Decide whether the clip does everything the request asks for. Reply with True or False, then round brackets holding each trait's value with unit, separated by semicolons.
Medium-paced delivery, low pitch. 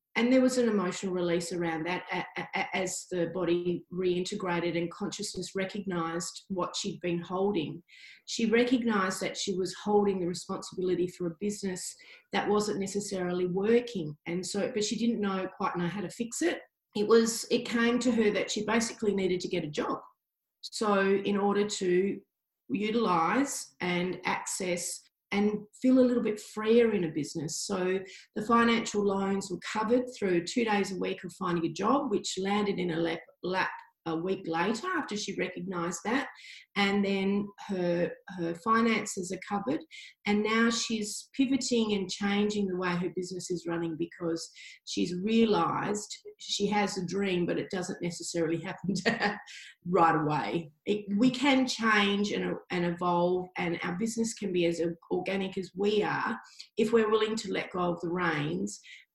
False (165 wpm; 195 Hz)